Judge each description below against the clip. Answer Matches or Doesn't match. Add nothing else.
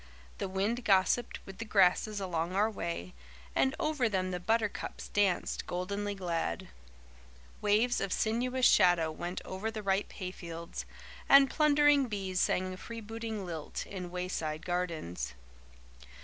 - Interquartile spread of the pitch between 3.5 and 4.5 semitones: Matches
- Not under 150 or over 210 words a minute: Doesn't match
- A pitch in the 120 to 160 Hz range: Doesn't match